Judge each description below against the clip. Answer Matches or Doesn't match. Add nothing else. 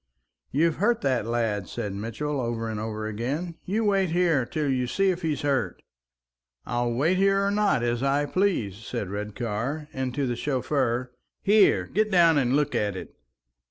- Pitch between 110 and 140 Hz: Matches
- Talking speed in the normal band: Matches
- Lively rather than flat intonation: Matches